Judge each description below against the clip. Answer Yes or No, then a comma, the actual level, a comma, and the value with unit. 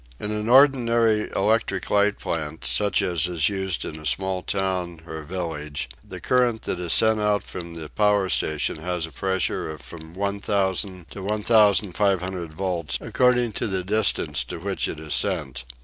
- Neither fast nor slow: Yes, average, 165 wpm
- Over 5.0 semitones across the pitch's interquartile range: No, average, 3.9 semitones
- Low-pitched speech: Yes, very low, 95 Hz